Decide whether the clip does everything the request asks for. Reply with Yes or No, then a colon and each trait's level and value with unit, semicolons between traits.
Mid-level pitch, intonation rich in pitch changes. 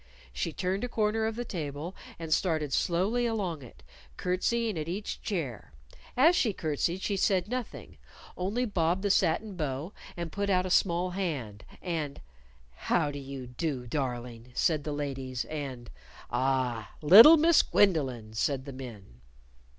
Yes: medium, 165 Hz; wide, 6.8 semitones